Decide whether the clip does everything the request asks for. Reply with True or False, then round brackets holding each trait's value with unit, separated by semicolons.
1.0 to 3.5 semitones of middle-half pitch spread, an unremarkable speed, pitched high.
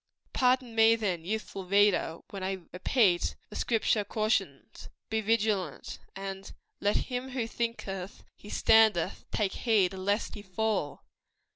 False (2.8 semitones; 130 wpm; 205 Hz)